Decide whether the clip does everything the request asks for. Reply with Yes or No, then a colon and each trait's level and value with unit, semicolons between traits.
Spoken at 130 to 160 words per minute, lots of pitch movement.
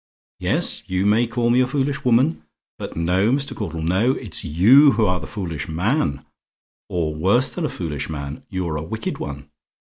No: average, 180 wpm; wide, 7.0 semitones